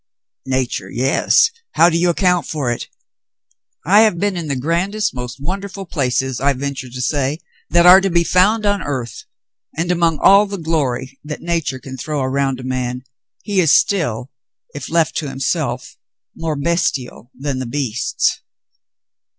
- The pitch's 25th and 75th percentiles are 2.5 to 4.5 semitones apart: No, average, 5.3 semitones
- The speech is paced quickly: No, average, 170 wpm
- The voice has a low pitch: No, medium, 150 Hz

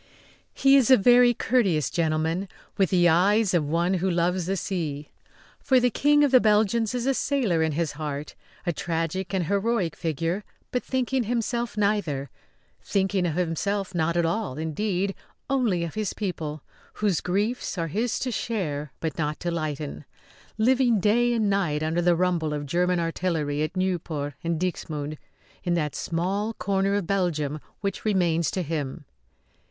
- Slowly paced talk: No, average, 165 wpm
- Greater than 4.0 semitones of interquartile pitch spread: Yes, average, 4.6 semitones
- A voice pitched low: No, medium, 180 Hz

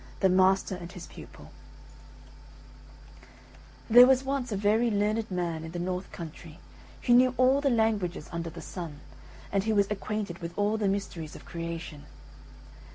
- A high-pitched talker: Yes, high, 195 Hz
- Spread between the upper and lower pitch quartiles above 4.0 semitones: Yes, average, 4.4 semitones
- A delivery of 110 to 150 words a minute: No, average, 160 wpm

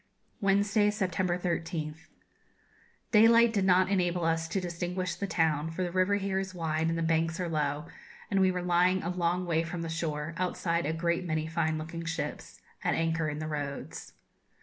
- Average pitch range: No, narrow, 2.3 semitones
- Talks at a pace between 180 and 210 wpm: Yes, average, 185 wpm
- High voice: No, medium, 170 Hz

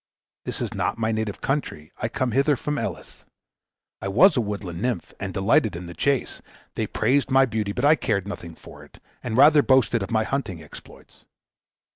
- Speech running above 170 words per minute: Yes, average, 190 wpm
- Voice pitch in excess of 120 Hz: No, low, 110 Hz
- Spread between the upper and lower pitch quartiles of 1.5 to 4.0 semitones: No, average, 5.3 semitones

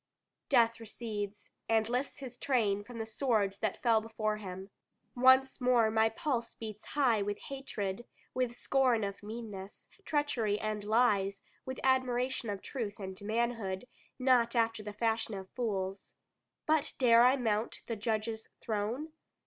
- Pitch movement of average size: Yes, average, 3.2 semitones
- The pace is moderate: Yes, average, 145 wpm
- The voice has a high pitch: Yes, high, 225 Hz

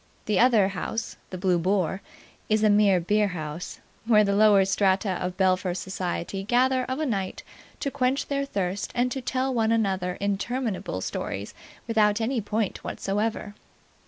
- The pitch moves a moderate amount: Yes, average, 3.4 semitones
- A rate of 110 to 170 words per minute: Yes, average, 155 wpm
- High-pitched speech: Yes, high, 205 Hz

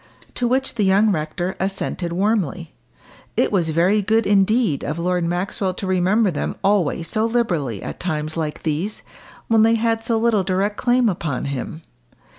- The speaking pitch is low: No, high, 190 Hz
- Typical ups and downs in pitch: Yes, average, 4.7 semitones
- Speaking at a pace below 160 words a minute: No, average, 165 wpm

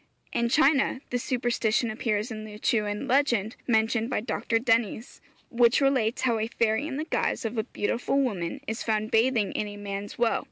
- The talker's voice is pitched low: No, high, 230 Hz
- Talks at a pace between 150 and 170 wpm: No, average, 190 wpm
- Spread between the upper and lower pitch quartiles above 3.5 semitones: No, narrow, 2.4 semitones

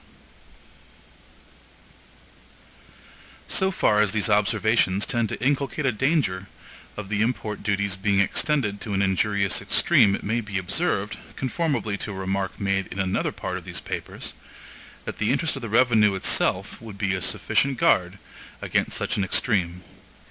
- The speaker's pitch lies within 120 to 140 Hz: No, low, 105 Hz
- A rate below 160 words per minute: Yes, average, 150 wpm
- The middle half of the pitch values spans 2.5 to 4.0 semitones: Yes, average, 3.3 semitones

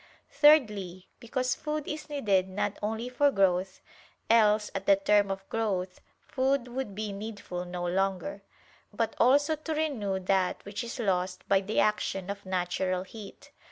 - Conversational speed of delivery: Yes, average, 155 wpm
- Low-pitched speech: No, high, 205 Hz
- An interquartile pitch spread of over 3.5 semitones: Yes, average, 4.3 semitones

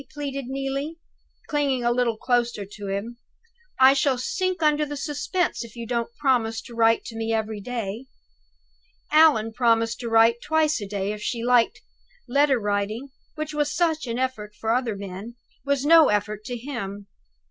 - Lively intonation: No, average, 4.2 semitones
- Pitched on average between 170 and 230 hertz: No, high, 240 Hz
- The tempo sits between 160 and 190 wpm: Yes, average, 170 wpm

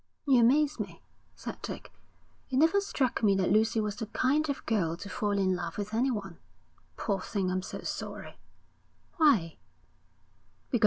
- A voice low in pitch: No, high, 215 Hz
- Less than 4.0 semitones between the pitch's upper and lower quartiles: No, wide, 5.5 semitones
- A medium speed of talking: Yes, average, 155 wpm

